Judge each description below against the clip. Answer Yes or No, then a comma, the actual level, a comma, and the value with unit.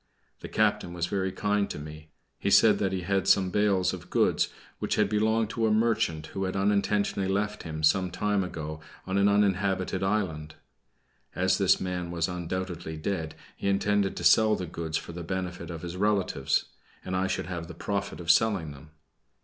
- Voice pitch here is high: No, very low, 95 Hz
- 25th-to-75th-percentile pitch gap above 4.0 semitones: No, average, 3.0 semitones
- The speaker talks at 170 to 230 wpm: Yes, average, 190 wpm